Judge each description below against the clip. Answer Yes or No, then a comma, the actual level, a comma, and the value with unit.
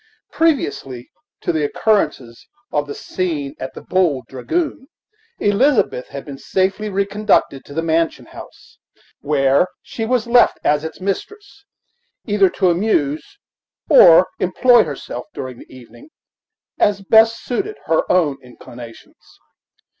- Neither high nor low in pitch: Yes, medium, 180 Hz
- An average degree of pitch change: No, wide, 7.8 semitones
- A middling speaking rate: No, slow, 125 wpm